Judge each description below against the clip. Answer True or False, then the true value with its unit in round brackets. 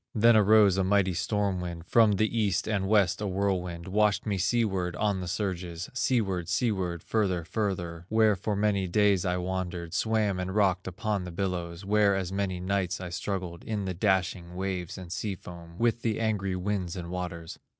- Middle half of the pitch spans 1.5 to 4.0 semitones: True (2.6 semitones)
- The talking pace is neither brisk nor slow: True (180 wpm)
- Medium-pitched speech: False (95 Hz)